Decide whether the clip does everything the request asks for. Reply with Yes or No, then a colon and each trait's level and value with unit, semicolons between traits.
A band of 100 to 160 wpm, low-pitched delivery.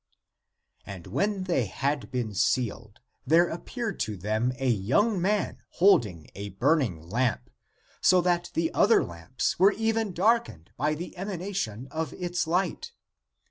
No: average, 140 wpm; medium, 155 Hz